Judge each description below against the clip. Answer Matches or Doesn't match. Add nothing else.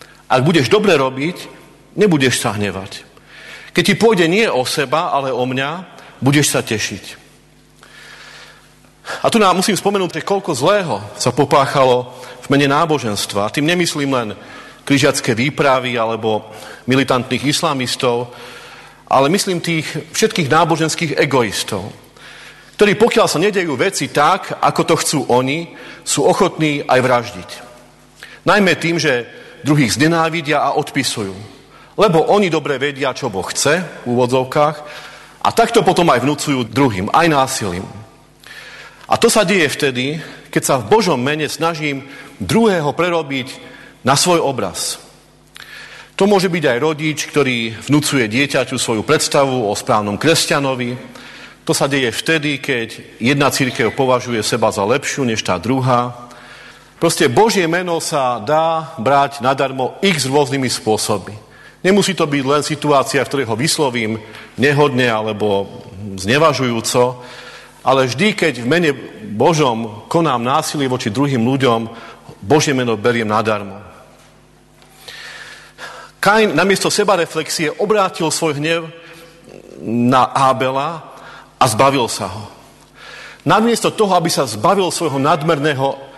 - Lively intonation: Doesn't match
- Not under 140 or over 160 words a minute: Doesn't match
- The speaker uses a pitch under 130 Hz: Doesn't match